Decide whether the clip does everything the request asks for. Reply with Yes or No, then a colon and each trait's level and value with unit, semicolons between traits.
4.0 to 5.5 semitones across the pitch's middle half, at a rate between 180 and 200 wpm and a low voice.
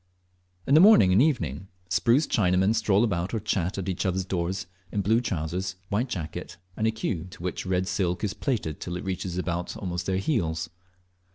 No: average, 3.5 semitones; average, 190 wpm; very low, 95 Hz